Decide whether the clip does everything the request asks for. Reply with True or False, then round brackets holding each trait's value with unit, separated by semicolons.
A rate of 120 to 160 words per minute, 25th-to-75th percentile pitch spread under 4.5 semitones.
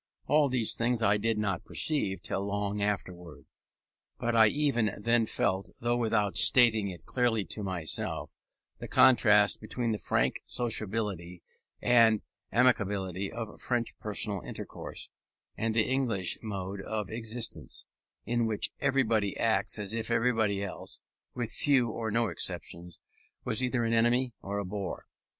True (140 wpm; 2.9 semitones)